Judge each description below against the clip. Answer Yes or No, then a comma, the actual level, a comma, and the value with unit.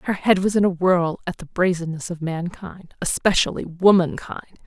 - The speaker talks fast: No, average, 165 wpm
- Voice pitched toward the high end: No, medium, 175 Hz